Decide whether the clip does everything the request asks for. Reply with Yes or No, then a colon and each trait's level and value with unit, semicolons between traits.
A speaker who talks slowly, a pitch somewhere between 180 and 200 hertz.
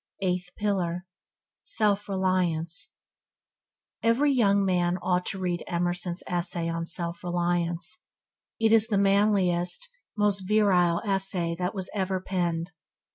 Yes: slow, 125 wpm; medium, 185 Hz